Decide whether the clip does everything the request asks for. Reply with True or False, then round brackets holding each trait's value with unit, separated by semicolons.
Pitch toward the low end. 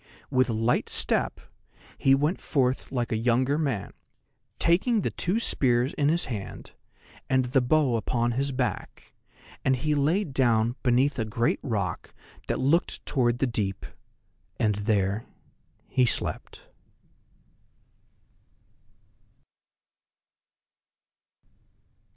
True (125 Hz)